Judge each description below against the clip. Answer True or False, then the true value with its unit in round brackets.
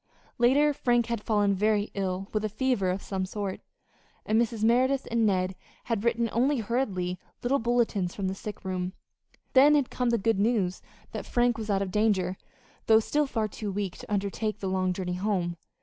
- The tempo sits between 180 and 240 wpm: True (190 wpm)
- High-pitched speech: True (215 Hz)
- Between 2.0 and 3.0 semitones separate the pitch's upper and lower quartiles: False (3.8 semitones)